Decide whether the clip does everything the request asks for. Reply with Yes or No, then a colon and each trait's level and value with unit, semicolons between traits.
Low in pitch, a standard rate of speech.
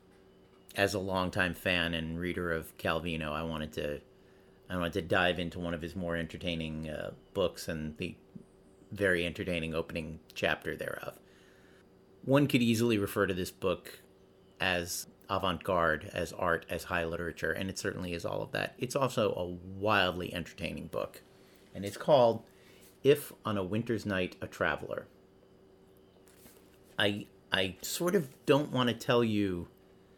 Yes: very low, 95 Hz; average, 150 wpm